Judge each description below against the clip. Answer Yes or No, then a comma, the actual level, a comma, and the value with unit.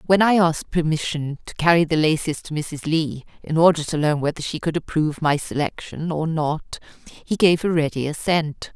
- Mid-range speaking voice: Yes, medium, 160 Hz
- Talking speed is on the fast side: No, average, 190 wpm